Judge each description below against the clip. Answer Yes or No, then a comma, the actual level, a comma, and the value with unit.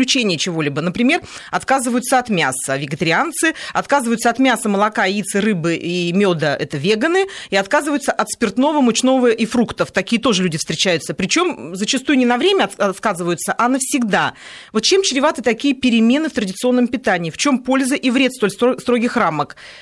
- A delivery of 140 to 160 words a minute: Yes, average, 155 wpm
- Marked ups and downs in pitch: Yes, wide, 5.7 semitones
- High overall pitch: Yes, high, 230 Hz